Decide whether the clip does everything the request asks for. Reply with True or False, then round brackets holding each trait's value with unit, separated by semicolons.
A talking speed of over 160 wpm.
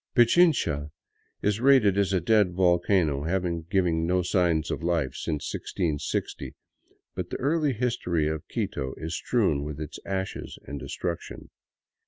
False (135 wpm)